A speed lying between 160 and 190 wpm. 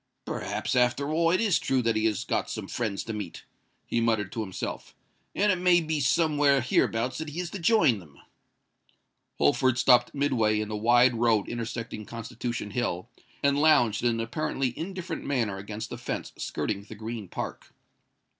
Yes: average, 175 wpm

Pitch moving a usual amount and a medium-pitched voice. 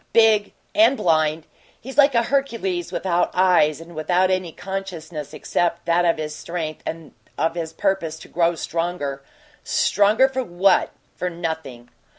Yes: average, 3.5 semitones; medium, 175 Hz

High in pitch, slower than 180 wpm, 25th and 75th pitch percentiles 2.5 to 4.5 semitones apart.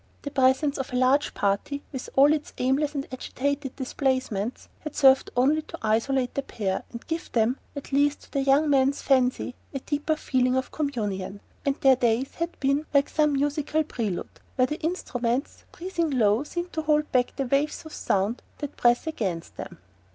No: very high, 270 Hz; average, 185 wpm; average, 2.9 semitones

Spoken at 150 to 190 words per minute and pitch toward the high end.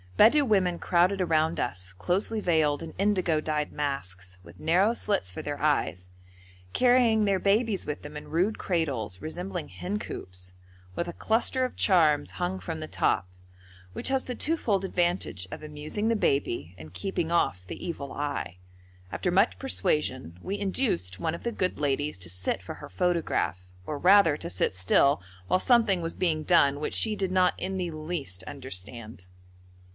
No: average, 170 wpm; medium, 160 Hz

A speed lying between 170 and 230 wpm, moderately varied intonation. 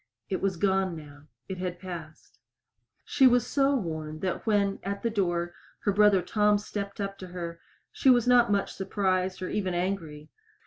Yes: average, 175 wpm; average, 3.0 semitones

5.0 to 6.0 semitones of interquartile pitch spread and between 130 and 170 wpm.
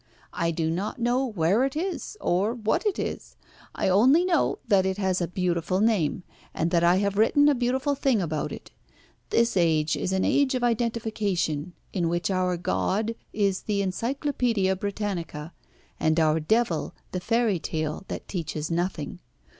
Yes: average, 5.3 semitones; average, 165 wpm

